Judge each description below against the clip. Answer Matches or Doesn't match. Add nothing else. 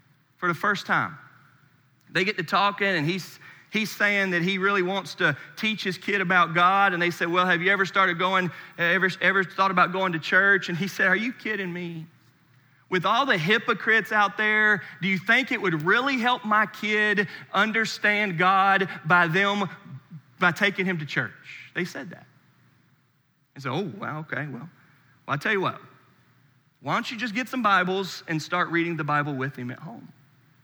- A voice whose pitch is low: Doesn't match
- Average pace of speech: Matches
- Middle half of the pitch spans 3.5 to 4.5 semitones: Matches